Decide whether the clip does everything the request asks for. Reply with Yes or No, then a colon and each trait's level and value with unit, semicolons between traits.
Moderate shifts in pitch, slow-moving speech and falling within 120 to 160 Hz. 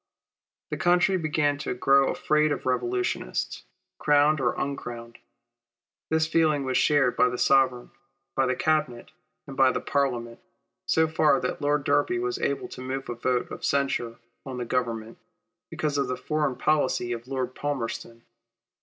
No: average, 3.5 semitones; average, 155 wpm; low, 135 Hz